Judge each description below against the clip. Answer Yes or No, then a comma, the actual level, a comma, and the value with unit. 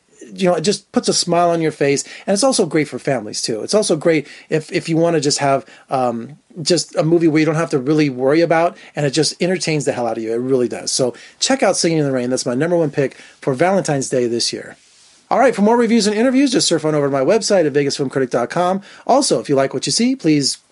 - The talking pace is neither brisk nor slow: No, fast, 265 wpm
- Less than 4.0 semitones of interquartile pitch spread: No, average, 4.7 semitones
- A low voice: No, medium, 155 Hz